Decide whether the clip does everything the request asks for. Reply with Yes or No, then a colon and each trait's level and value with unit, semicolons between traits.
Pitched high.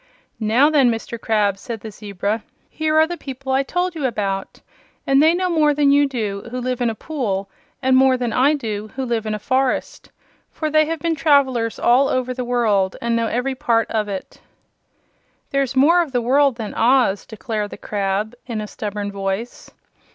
Yes: high, 245 Hz